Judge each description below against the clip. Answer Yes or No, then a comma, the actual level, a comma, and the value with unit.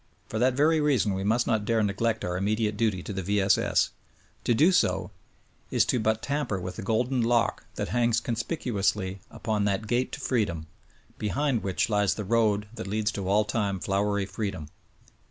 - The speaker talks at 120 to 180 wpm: No, average, 190 wpm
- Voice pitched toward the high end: No, low, 110 Hz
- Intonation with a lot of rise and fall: No, average, 2.9 semitones